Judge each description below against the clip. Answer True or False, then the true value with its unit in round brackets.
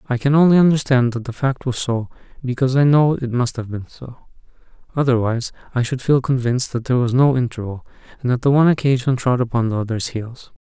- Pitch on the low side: True (125 Hz)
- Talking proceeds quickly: True (210 wpm)